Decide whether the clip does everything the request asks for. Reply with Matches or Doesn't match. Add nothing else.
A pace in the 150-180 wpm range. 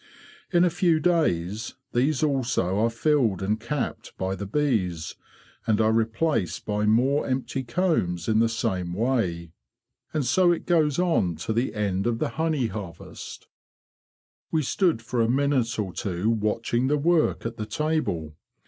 Matches